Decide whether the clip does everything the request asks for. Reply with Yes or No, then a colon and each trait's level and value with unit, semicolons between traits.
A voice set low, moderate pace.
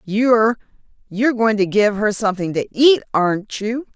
No: high, 215 Hz; average, 150 wpm